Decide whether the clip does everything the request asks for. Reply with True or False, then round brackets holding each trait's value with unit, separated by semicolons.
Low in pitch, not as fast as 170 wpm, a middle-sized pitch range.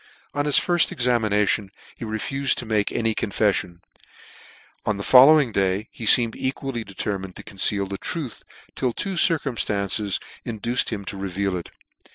True (110 Hz; 155 wpm; 4.2 semitones)